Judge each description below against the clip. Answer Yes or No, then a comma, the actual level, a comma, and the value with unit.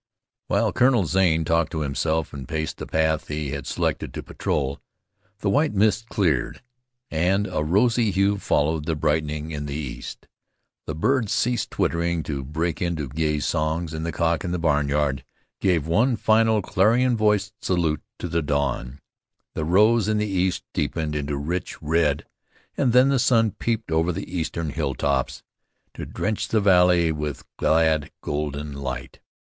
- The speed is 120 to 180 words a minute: Yes, average, 160 wpm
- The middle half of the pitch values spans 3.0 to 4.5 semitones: No, average, 4.9 semitones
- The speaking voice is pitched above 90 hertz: No, very low, 80 Hz